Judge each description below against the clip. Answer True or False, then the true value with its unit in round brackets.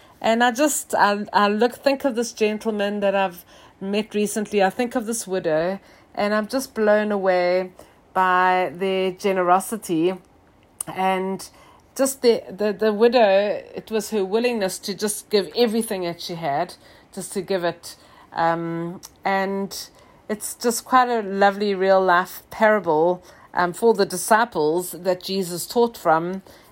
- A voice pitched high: True (195 Hz)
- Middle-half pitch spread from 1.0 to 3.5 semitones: True (3.1 semitones)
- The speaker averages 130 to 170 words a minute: True (150 wpm)